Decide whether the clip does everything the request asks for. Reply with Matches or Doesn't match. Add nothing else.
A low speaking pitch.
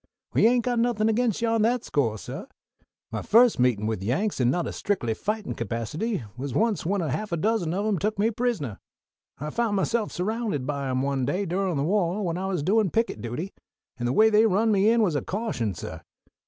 Doesn't match